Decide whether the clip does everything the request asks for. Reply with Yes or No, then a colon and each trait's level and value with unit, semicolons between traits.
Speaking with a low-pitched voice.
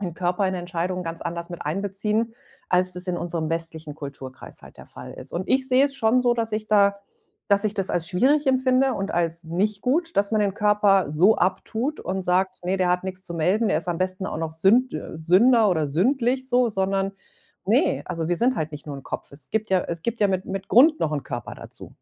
No: high, 190 Hz